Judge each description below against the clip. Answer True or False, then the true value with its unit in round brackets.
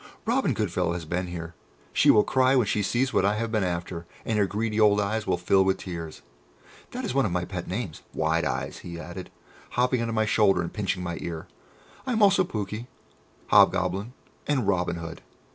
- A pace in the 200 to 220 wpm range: True (205 wpm)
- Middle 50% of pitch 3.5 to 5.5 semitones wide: True (4.5 semitones)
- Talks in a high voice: False (100 Hz)